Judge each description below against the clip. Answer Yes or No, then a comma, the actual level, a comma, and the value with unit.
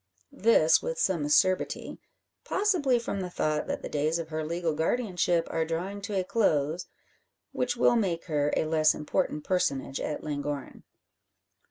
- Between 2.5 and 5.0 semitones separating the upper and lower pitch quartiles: Yes, average, 4.1 semitones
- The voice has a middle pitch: Yes, medium, 165 Hz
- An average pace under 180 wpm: Yes, average, 155 wpm